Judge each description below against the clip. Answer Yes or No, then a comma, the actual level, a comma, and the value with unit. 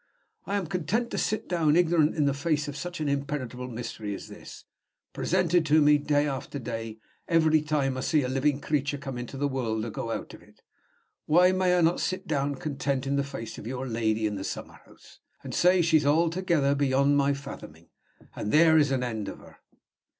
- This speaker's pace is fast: Yes, fast, 210 wpm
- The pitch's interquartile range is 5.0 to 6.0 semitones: No, average, 3.6 semitones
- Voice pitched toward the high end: No, medium, 145 Hz